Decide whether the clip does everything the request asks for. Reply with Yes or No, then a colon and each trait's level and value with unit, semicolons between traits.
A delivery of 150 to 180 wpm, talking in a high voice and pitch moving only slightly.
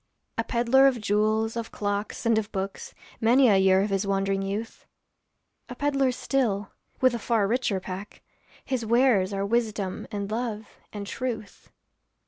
No: average, 155 wpm; high, 215 Hz; average, 3.2 semitones